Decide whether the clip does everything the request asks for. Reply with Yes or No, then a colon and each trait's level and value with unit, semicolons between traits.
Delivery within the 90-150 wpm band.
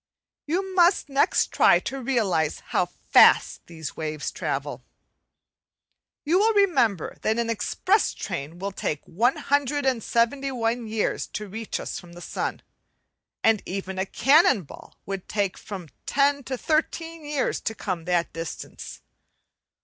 Yes: slow, 135 wpm